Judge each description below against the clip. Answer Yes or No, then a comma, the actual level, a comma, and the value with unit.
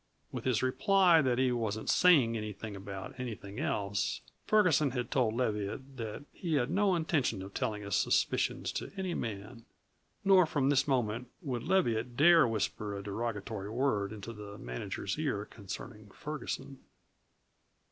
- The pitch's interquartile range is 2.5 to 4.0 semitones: No, average, 5.2 semitones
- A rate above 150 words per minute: No, average, 145 wpm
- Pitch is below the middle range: Yes, low, 120 Hz